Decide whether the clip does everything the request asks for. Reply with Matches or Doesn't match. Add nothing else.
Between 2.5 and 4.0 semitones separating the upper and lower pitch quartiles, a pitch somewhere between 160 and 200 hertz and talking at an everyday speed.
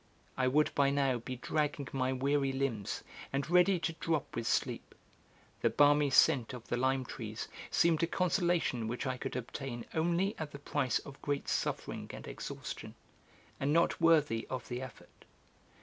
Doesn't match